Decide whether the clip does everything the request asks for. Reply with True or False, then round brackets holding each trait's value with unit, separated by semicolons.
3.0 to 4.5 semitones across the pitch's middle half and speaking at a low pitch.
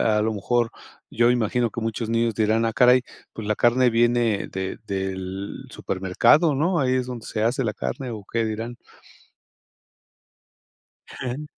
False (2.5 semitones; 115 Hz)